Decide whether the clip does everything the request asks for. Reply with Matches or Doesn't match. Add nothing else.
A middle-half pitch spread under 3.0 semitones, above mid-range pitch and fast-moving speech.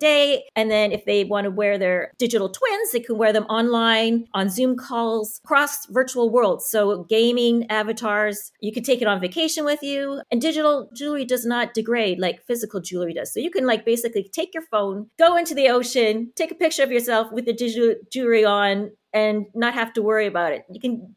Doesn't match